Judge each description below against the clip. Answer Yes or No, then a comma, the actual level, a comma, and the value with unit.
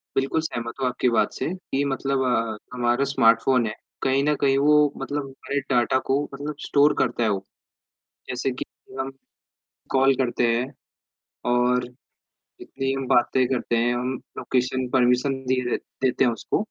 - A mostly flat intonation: Yes, narrow, 2.0 semitones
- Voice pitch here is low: Yes, low, 130 Hz